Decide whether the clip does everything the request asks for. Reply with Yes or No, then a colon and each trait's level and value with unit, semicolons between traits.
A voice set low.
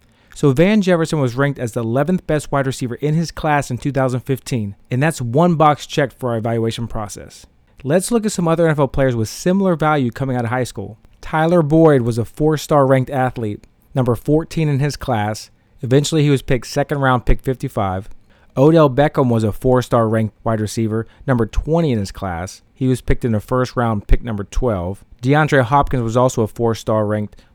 Yes: low, 130 Hz